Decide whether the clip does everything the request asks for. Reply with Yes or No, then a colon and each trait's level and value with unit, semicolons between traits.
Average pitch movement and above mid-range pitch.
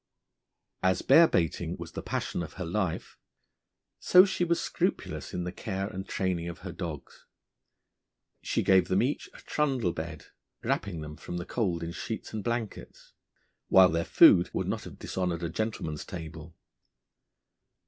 No: average, 4.3 semitones; very low, 90 Hz